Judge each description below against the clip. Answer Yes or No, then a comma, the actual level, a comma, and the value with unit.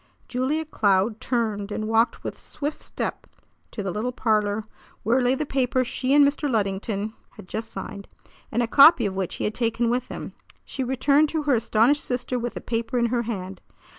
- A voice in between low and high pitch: No, high, 235 Hz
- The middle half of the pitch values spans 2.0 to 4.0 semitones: Yes, average, 3.4 semitones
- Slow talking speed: No, average, 195 wpm